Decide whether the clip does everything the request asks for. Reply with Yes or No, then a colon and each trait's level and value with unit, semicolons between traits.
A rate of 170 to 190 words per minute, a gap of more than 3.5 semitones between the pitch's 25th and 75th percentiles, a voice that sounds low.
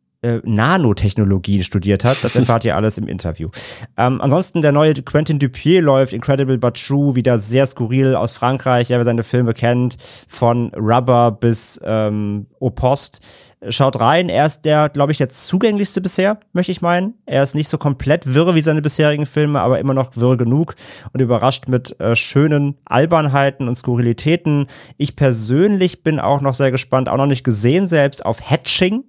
Yes: average, 175 wpm; average, 3.9 semitones; low, 130 Hz